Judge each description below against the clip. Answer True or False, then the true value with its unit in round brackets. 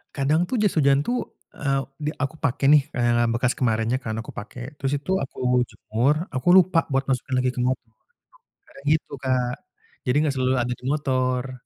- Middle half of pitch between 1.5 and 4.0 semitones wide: True (2.5 semitones)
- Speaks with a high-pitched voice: False (130 Hz)